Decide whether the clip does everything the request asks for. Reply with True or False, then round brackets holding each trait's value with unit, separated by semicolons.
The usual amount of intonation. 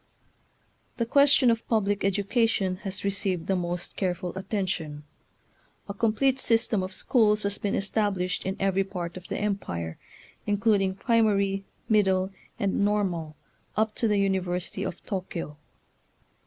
False (2.3 semitones)